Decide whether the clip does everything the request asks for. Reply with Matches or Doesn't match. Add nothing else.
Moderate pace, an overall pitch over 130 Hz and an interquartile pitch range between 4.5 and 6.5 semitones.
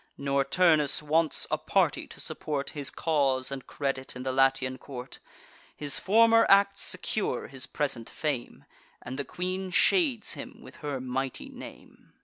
Matches